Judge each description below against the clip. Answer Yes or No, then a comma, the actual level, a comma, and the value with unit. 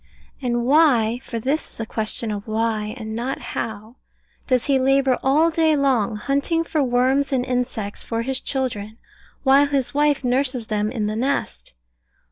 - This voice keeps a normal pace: Yes, average, 170 wpm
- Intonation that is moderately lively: Yes, average, 3.9 semitones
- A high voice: Yes, very high, 250 Hz